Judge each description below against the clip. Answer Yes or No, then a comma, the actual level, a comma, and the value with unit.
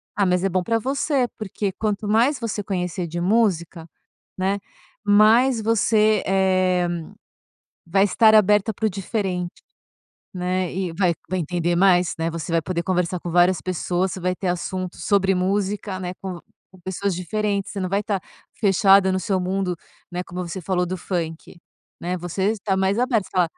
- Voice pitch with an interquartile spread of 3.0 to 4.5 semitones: No, narrow, 2.4 semitones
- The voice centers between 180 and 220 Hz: Yes, high, 190 Hz